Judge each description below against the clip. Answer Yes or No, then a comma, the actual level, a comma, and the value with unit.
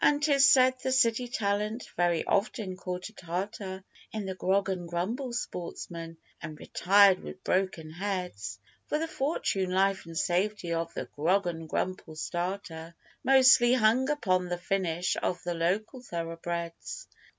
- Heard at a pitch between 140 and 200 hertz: Yes, high, 190 Hz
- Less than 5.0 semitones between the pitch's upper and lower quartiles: Yes, average, 4.3 semitones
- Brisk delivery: No, average, 150 wpm